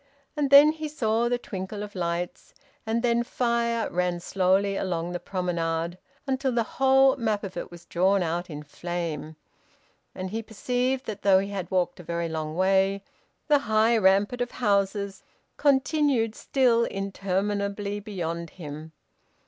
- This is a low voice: No, high, 200 Hz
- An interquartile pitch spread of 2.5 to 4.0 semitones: No, average, 4.8 semitones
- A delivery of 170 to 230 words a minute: No, average, 150 wpm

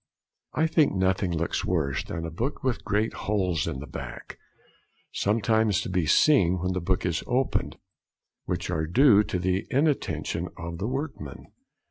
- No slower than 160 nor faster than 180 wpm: Yes, average, 165 wpm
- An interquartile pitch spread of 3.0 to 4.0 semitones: No, wide, 5.5 semitones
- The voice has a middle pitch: No, very low, 95 Hz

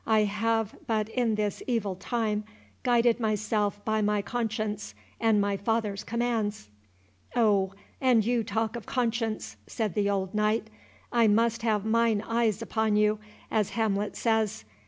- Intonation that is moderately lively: No, narrow, 1.7 semitones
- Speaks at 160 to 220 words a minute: No, average, 145 wpm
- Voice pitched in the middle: No, high, 220 Hz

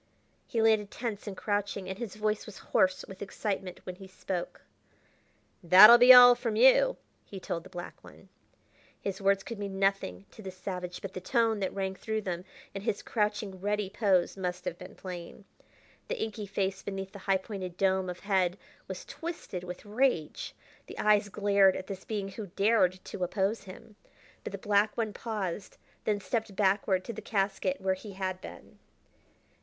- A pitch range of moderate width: No, narrow, 2.1 semitones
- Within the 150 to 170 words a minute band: No, average, 180 wpm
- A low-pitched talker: No, high, 195 Hz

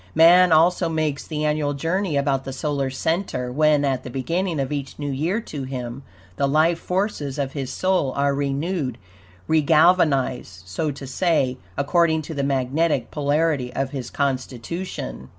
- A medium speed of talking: Yes, average, 155 wpm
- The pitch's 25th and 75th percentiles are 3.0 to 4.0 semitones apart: Yes, average, 3.4 semitones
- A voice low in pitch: No, medium, 145 Hz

